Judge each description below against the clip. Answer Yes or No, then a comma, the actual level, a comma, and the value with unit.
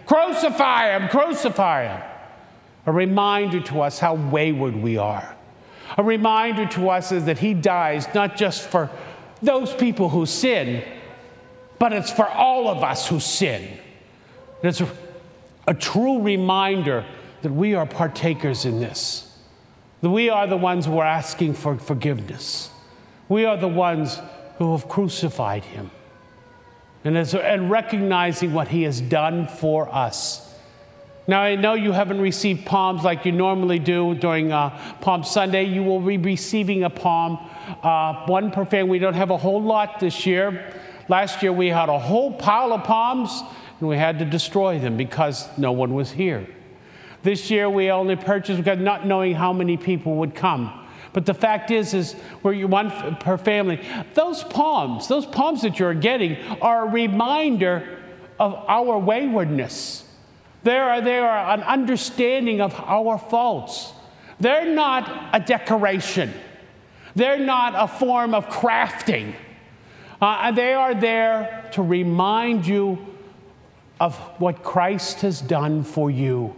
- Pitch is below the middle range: No, medium, 185 Hz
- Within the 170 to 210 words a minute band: No, average, 155 wpm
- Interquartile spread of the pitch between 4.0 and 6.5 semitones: Yes, average, 4.9 semitones